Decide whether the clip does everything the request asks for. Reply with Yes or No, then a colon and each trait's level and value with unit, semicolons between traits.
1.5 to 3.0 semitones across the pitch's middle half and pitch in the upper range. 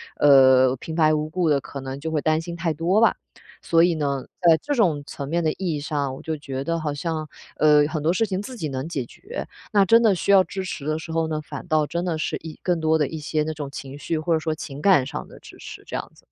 No: average, 2.7 semitones; medium, 155 Hz